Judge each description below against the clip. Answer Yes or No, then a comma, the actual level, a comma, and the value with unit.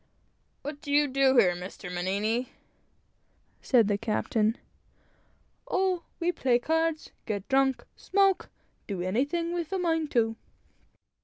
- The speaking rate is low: Yes, slow, 125 wpm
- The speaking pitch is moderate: No, very high, 265 Hz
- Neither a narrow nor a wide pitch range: No, wide, 7.2 semitones